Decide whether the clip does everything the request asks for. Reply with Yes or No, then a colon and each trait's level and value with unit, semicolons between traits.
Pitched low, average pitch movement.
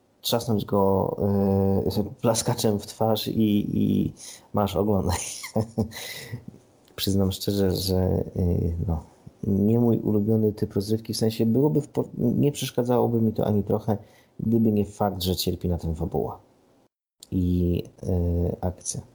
Yes: low, 105 Hz; average, 3.1 semitones